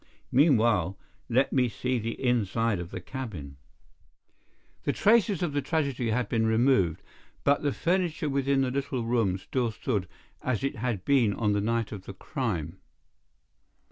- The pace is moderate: Yes, average, 155 wpm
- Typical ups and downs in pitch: Yes, average, 4.8 semitones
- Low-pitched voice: Yes, low, 120 Hz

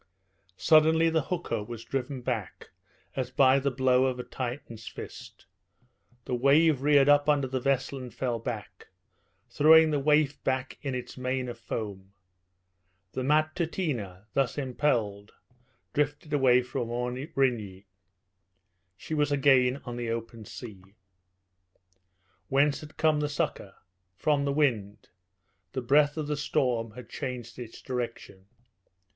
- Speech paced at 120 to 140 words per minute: Yes, slow, 135 wpm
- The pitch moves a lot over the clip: No, average, 3.6 semitones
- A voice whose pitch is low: Yes, low, 130 Hz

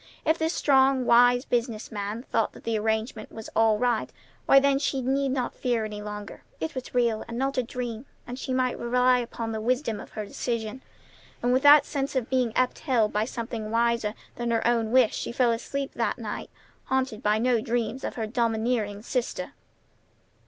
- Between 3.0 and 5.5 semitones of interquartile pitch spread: No, narrow, 2.6 semitones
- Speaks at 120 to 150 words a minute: No, average, 190 wpm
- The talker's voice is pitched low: No, high, 240 Hz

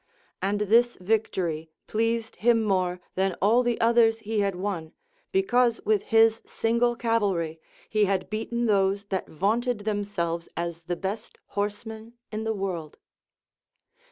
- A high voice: Yes, high, 210 Hz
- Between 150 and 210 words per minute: No, slow, 135 wpm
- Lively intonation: No, average, 3.1 semitones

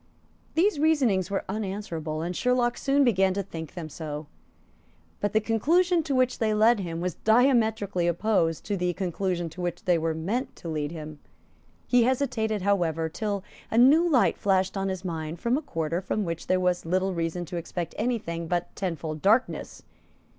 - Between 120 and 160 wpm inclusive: No, average, 180 wpm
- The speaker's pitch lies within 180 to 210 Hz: Yes, high, 190 Hz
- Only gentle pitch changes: No, average, 5.2 semitones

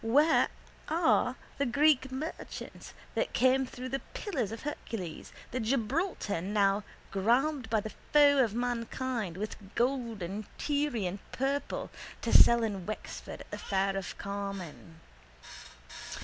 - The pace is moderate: No, slow, 130 wpm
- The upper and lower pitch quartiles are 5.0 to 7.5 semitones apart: Yes, average, 5.3 semitones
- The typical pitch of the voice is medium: No, high, 235 Hz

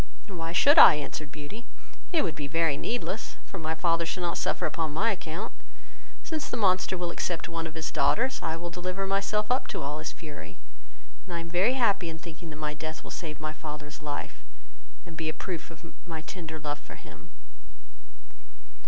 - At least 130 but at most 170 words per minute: No, average, 200 wpm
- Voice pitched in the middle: Yes, medium, 165 Hz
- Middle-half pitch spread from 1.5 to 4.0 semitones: Yes, average, 3.3 semitones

